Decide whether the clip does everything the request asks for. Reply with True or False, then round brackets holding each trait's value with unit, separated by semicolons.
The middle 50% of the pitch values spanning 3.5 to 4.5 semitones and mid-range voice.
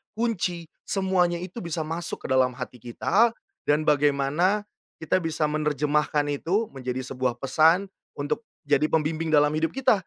True (3.8 semitones; 155 Hz)